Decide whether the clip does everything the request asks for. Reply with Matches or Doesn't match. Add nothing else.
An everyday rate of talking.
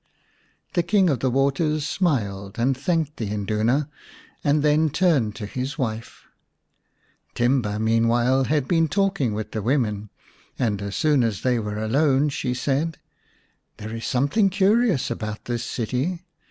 Matches